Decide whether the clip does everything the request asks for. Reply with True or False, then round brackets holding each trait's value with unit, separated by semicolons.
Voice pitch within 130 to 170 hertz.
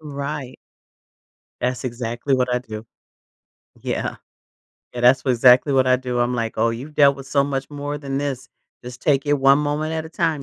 True (135 Hz)